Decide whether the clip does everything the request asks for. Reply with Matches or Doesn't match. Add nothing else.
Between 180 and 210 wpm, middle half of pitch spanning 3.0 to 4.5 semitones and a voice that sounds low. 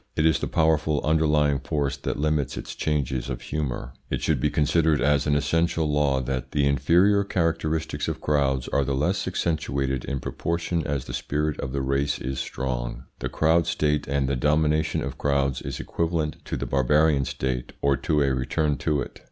Doesn't match